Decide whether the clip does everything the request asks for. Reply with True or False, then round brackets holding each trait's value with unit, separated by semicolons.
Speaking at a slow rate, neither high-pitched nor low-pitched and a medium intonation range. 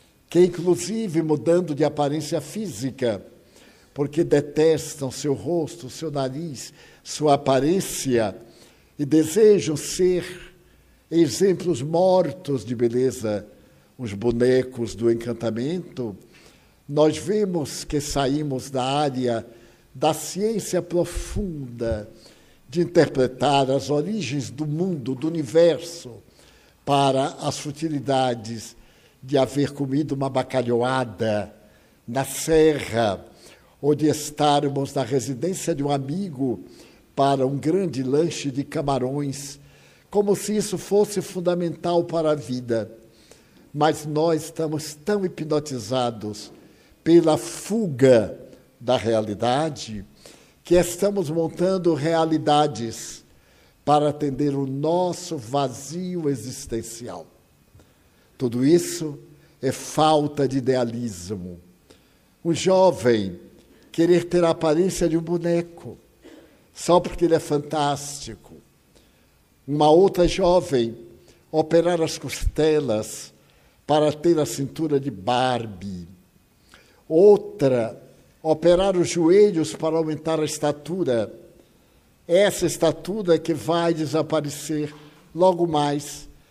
True (100 wpm; 150 Hz; 4.6 semitones)